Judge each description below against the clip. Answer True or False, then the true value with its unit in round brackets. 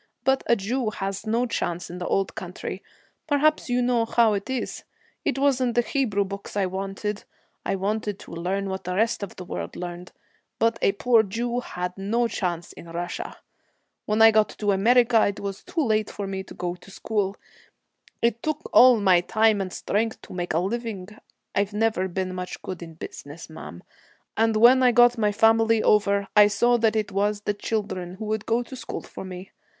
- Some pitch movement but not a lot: True (3.4 semitones)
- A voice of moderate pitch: False (210 Hz)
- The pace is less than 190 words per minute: False (195 wpm)